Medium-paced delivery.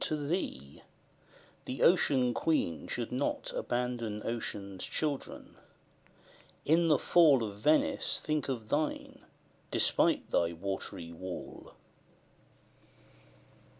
No: slow, 95 wpm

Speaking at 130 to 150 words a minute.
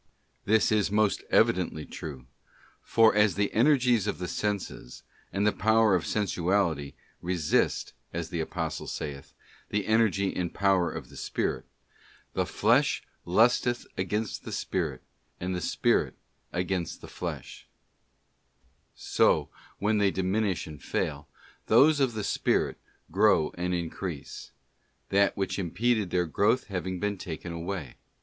Yes: average, 140 wpm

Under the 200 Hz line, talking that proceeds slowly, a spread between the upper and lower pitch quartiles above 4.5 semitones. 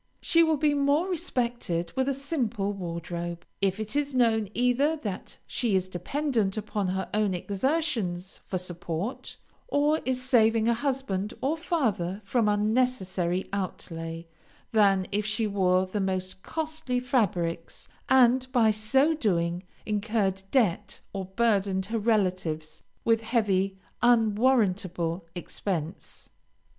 No: high, 210 Hz; slow, 125 wpm; average, 5.2 semitones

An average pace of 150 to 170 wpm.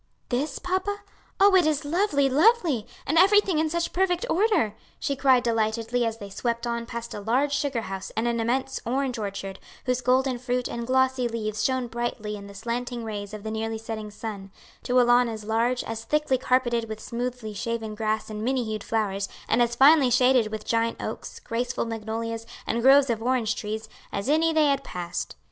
No: average, 195 wpm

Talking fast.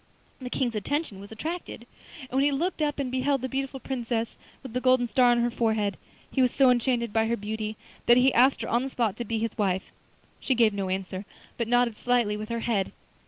Yes: fast, 225 wpm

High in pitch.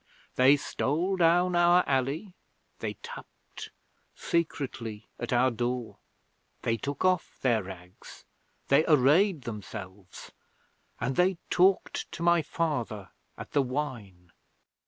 No: medium, 140 Hz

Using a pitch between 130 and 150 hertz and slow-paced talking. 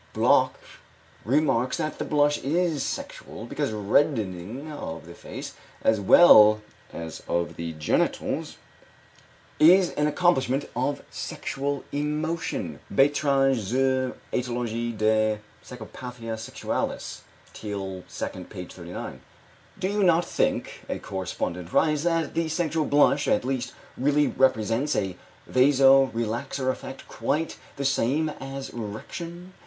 Yes: low, 135 Hz; slow, 115 wpm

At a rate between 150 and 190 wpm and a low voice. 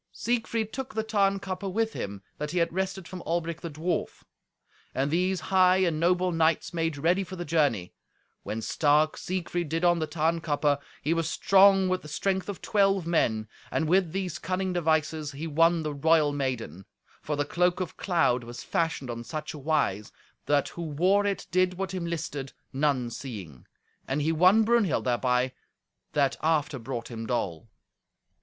No: average, 170 wpm; medium, 165 Hz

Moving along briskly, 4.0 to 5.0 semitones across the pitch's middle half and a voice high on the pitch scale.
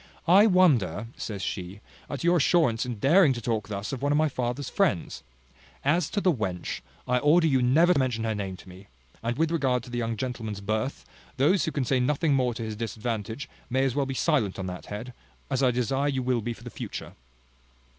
No: fast, 220 wpm; average, 4.6 semitones; low, 125 Hz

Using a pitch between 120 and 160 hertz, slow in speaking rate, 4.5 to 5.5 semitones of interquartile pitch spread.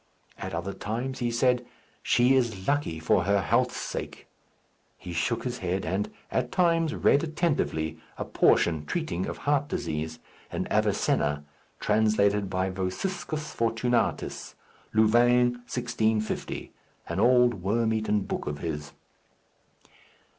No: low, 110 Hz; slow, 125 wpm; average, 5.1 semitones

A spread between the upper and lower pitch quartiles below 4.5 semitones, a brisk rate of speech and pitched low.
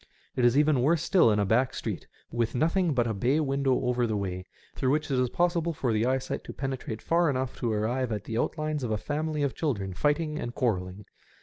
No: average, 5.1 semitones; fast, 225 wpm; low, 130 Hz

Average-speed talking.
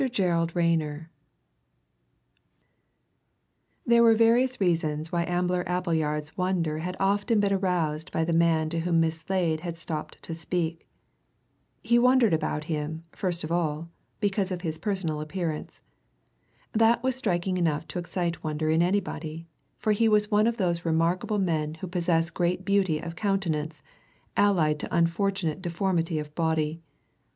Yes: average, 145 wpm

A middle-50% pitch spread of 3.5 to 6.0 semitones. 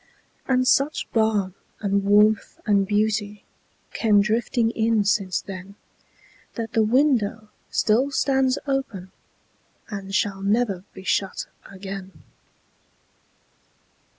No: average, 2.7 semitones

